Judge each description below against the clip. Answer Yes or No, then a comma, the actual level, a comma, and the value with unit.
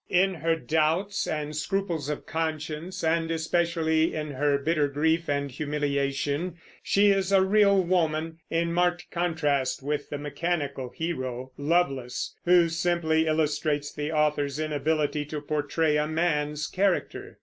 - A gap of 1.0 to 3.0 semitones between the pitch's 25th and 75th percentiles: Yes, narrow, 2.6 semitones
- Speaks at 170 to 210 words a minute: No, slow, 135 wpm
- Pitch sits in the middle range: Yes, medium, 155 Hz